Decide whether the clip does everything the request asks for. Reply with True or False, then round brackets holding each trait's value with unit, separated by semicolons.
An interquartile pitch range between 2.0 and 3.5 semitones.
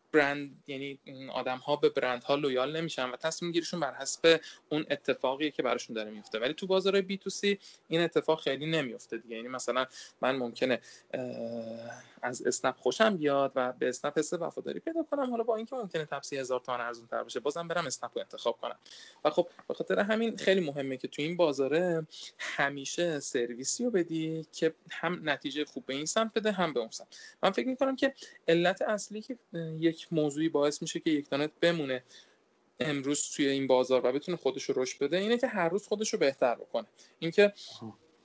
False (4.9 semitones)